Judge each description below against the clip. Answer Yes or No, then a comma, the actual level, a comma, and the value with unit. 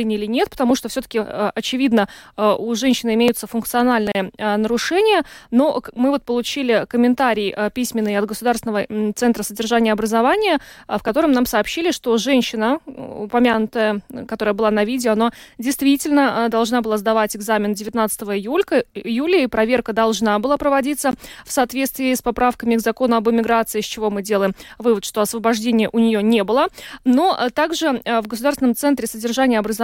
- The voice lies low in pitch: No, high, 230 Hz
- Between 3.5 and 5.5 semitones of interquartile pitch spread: No, average, 3.1 semitones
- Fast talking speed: No, average, 145 wpm